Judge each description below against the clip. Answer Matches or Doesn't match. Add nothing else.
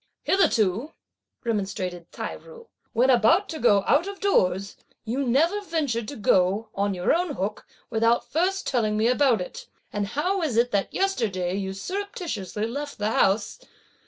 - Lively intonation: Matches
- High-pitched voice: Matches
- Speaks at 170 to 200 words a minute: Doesn't match